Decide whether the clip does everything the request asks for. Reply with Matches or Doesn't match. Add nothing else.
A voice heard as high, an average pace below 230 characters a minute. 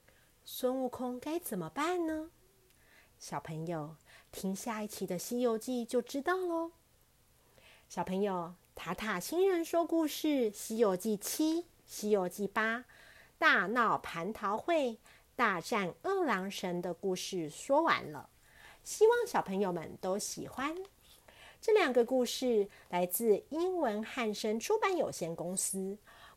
Matches